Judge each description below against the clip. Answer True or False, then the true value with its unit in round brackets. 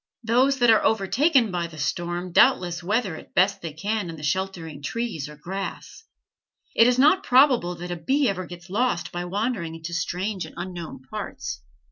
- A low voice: False (185 Hz)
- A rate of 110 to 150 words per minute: False (185 wpm)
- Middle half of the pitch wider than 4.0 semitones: True (5.1 semitones)